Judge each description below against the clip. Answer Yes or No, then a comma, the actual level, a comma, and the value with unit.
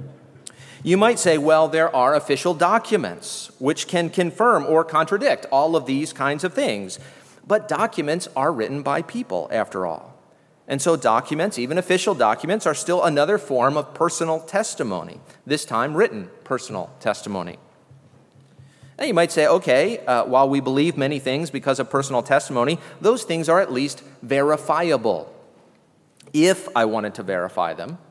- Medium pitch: Yes, medium, 155 Hz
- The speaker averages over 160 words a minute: No, average, 155 wpm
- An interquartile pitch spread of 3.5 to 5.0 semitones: Yes, average, 4.6 semitones